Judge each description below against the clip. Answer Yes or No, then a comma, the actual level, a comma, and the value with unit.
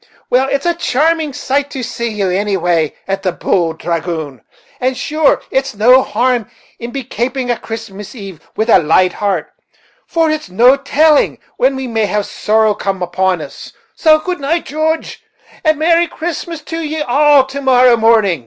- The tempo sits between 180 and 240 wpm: No, average, 170 wpm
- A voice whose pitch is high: Yes, high, 245 Hz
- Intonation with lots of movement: Yes, wide, 7.0 semitones